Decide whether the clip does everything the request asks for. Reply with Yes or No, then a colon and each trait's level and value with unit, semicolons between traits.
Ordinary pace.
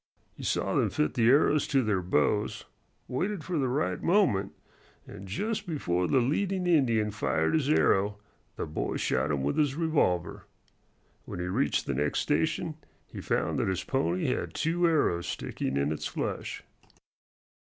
Yes: average, 165 wpm